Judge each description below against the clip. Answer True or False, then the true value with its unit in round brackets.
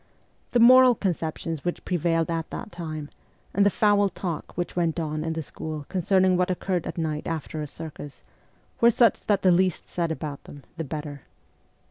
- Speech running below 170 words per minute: False (185 wpm)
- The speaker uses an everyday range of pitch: True (3.3 semitones)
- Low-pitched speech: False (170 Hz)